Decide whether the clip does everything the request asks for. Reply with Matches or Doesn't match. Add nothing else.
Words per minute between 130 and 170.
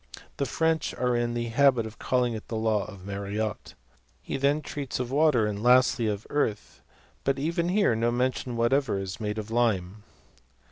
Doesn't match